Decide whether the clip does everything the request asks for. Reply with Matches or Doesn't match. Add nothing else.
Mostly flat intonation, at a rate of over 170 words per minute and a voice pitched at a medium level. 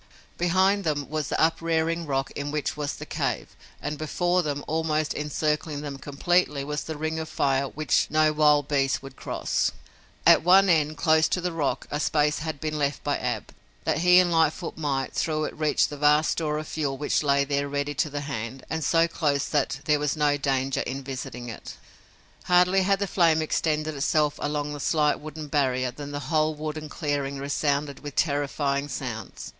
Matches